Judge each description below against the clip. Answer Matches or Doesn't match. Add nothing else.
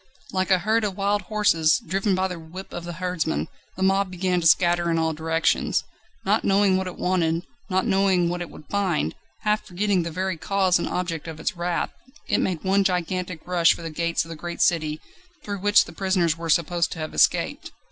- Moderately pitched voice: Matches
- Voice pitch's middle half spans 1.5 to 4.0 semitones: Matches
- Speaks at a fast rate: Matches